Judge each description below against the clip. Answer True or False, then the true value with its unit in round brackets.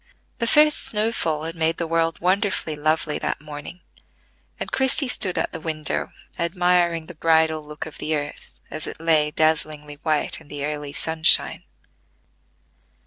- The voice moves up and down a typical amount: False (2.3 semitones)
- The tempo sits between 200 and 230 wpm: False (155 wpm)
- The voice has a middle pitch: True (160 Hz)